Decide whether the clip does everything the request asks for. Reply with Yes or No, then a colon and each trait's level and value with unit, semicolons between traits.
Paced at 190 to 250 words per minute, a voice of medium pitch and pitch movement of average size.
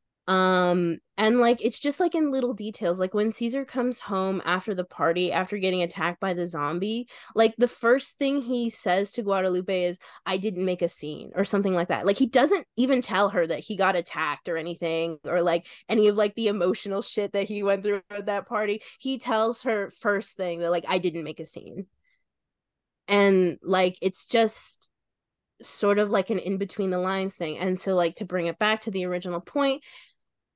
No: fast, 205 wpm; high, 195 Hz; average, 3.7 semitones